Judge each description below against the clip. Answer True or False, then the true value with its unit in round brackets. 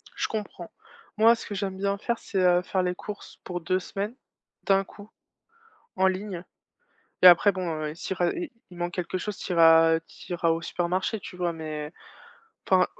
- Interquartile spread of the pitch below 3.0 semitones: True (2.5 semitones)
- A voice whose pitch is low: False (185 Hz)